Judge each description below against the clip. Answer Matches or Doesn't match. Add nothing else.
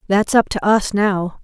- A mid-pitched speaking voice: Doesn't match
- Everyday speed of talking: Doesn't match